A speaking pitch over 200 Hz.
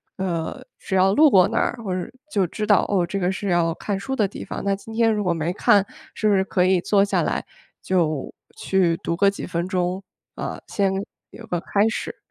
No: high, 190 Hz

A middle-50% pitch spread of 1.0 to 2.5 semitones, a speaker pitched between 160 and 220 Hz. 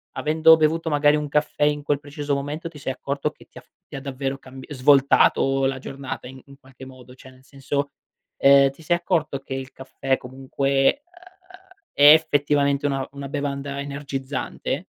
No: narrow, 1.5 semitones; medium, 140 Hz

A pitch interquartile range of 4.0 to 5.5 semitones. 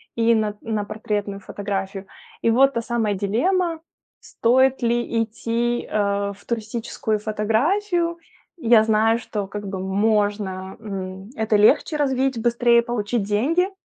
No: average, 2.7 semitones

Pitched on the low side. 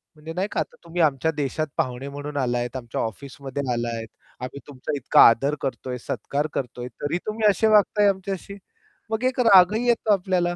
No: medium, 150 Hz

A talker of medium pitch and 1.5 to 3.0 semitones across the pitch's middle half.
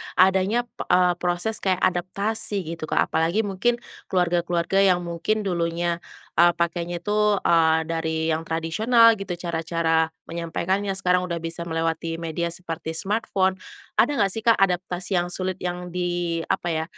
Yes: medium, 175 Hz; narrow, 2.4 semitones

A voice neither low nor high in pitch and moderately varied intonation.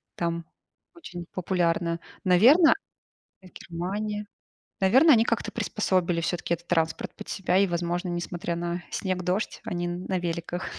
No: medium, 175 Hz; narrow, 1.9 semitones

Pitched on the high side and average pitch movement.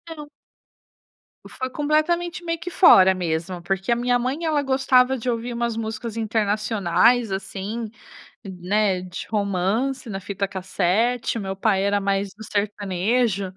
Yes: high, 215 Hz; average, 4.3 semitones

